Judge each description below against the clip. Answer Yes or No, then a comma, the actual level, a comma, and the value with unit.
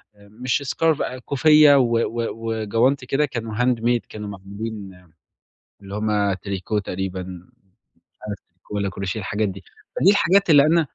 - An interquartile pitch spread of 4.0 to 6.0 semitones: Yes, average, 4.5 semitones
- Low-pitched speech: Yes, low, 110 Hz